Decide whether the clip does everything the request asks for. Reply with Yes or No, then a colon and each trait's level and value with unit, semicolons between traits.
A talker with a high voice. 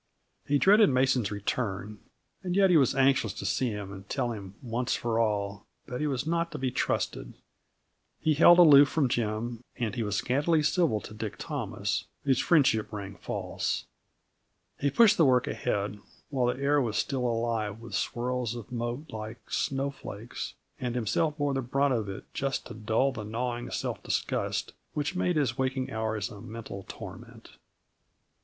No: low, 125 Hz